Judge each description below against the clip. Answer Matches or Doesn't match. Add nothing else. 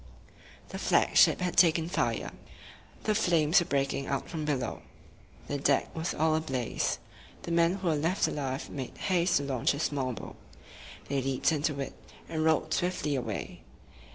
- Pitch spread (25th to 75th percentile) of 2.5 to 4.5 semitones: Matches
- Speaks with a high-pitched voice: Doesn't match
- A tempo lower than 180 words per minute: Matches